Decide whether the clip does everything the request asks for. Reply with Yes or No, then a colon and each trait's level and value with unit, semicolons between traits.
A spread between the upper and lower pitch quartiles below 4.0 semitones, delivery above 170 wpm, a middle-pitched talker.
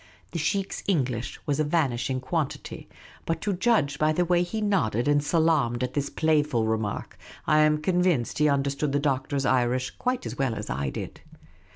No: average, 4.4 semitones; average, 180 wpm; medium, 145 Hz